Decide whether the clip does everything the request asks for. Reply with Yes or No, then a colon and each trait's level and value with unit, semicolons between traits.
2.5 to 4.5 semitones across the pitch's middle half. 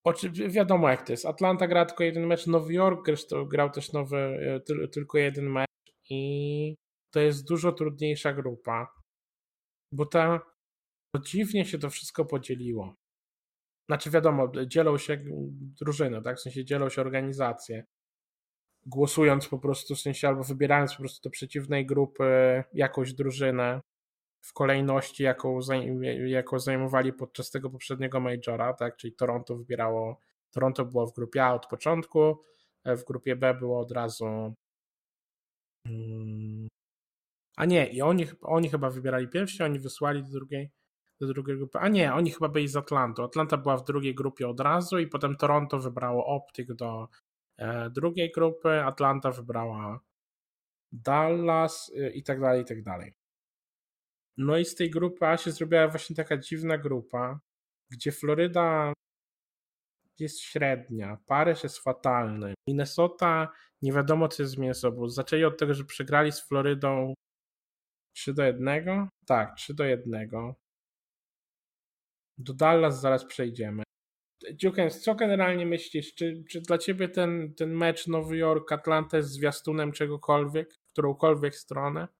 Yes: average, 3.6 semitones